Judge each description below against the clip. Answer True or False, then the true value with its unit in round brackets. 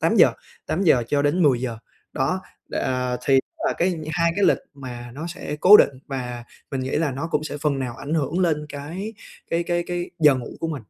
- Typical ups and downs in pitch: True (4.3 semitones)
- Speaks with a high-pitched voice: False (145 Hz)